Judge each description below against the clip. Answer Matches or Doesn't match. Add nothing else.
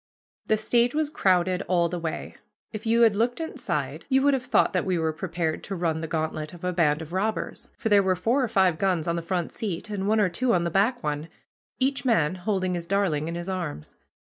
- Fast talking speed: Matches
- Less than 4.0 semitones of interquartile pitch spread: Doesn't match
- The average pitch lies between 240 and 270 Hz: Doesn't match